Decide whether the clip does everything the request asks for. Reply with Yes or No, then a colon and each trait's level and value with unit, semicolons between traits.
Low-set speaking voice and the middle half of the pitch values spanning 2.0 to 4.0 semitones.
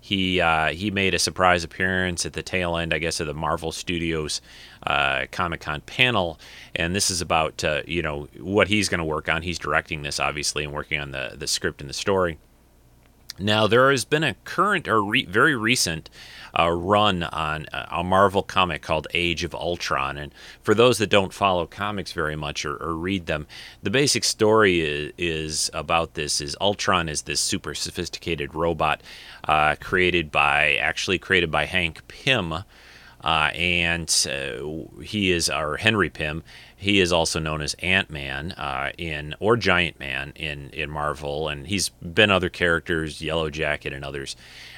Yes: very low, 85 Hz; average, 3.6 semitones